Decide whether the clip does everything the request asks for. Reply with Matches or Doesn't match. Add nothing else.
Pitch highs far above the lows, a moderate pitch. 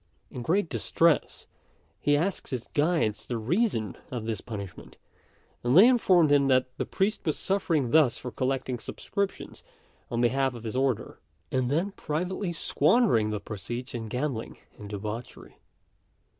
Doesn't match